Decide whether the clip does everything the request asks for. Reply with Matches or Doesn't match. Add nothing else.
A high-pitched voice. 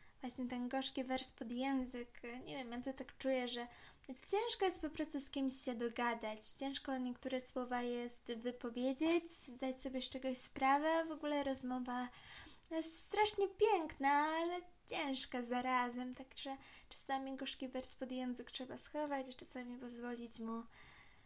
Matches